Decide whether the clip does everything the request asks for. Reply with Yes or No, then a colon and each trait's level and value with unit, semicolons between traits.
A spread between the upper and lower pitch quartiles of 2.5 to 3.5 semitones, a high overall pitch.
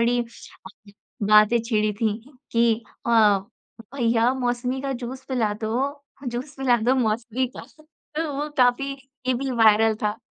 Yes: average, 2.9 semitones; high, 240 Hz